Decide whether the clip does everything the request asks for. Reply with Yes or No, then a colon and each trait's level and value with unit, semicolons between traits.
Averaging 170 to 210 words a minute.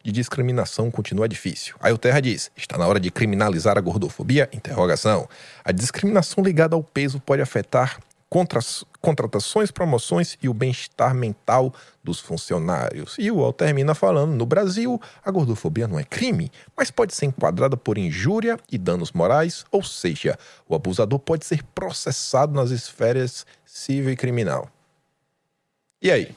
No: average, 150 wpm